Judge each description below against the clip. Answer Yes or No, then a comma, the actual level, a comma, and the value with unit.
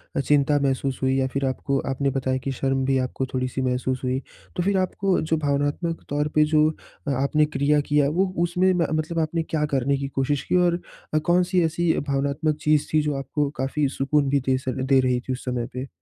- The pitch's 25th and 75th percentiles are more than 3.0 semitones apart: No, average, 2.7 semitones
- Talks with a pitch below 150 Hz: Yes, medium, 140 Hz